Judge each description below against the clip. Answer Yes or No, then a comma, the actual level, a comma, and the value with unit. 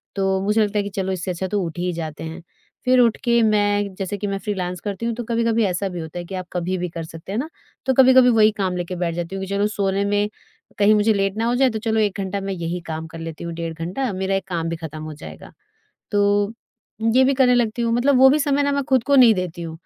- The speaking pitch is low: No, high, 195 Hz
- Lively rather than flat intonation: No, average, 4.4 semitones